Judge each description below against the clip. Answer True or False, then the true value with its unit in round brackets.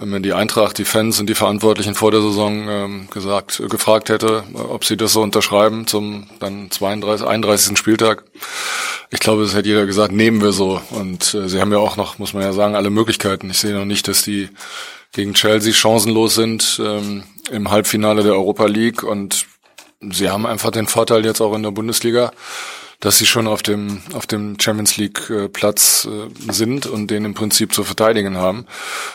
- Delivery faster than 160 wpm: True (185 wpm)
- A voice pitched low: True (105 Hz)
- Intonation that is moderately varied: False (1.4 semitones)